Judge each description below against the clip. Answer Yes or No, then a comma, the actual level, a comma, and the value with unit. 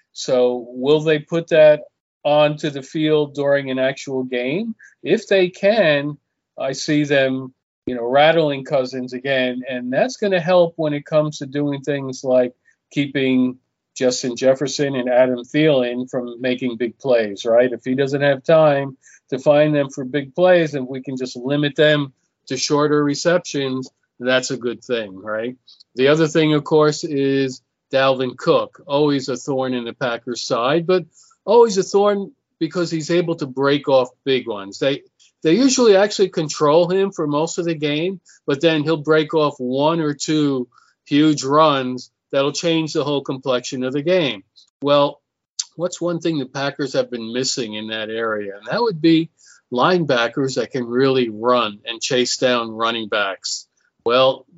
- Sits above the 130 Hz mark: Yes, medium, 140 Hz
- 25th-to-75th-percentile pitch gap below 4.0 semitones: Yes, average, 3.5 semitones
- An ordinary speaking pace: Yes, average, 170 wpm